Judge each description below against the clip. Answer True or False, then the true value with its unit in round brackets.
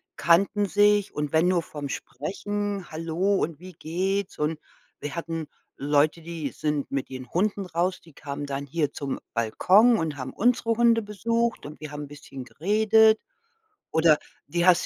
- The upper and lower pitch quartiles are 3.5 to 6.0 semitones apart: True (5.4 semitones)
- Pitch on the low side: False (170 Hz)